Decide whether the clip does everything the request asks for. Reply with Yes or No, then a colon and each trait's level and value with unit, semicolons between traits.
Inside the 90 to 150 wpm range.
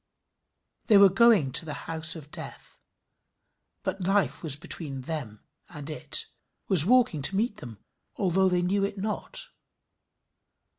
Yes: average, 140 wpm